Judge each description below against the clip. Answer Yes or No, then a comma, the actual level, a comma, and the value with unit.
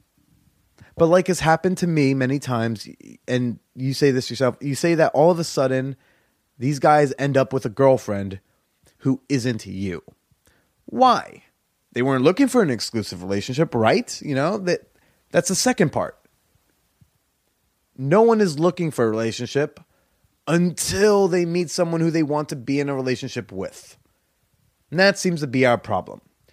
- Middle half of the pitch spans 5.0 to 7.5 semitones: Yes, wide, 5.6 semitones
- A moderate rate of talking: Yes, average, 165 wpm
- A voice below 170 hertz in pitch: Yes, medium, 140 Hz